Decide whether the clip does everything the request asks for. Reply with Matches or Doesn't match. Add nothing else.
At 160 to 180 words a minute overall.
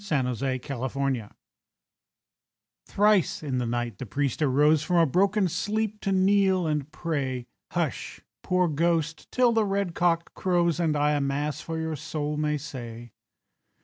Doesn't match